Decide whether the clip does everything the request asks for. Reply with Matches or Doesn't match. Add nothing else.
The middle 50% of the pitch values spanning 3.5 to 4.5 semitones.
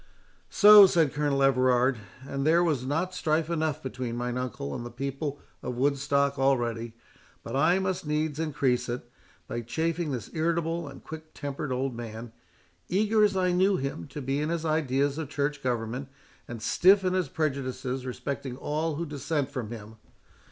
Matches